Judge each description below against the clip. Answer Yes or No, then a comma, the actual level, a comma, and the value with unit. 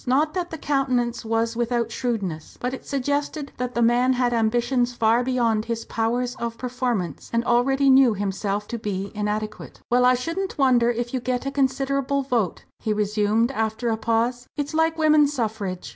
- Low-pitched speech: No, high, 240 Hz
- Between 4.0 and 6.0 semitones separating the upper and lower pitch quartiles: No, average, 2.9 semitones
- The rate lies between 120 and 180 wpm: Yes, average, 175 wpm